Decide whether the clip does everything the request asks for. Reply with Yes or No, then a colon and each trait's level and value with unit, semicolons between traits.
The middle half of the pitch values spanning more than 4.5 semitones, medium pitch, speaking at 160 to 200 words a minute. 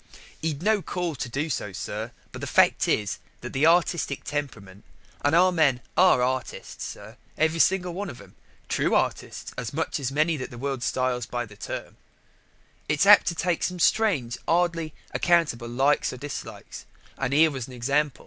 Yes: average, 5.2 semitones; medium, 145 Hz; average, 175 wpm